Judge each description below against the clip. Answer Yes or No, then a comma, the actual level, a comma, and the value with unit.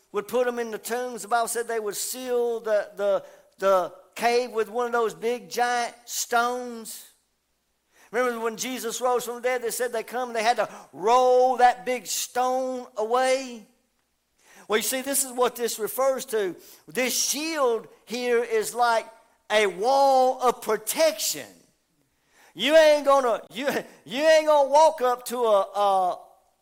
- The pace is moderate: Yes, average, 165 wpm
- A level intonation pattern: Yes, narrow, 2.2 semitones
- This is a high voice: Yes, high, 245 Hz